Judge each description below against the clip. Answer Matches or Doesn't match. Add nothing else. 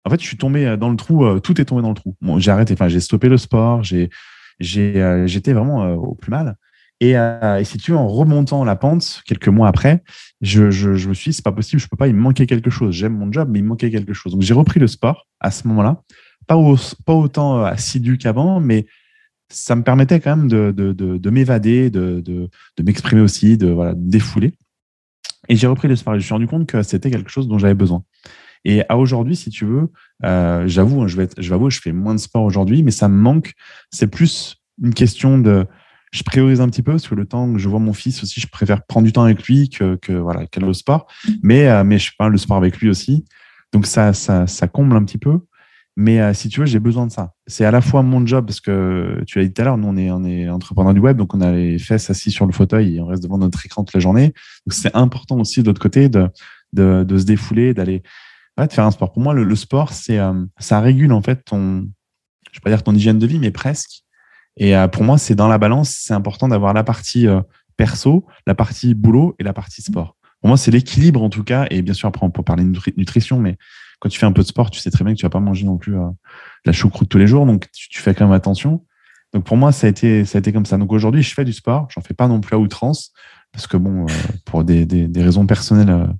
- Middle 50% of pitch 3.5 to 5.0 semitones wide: Matches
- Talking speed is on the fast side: Matches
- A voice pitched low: Matches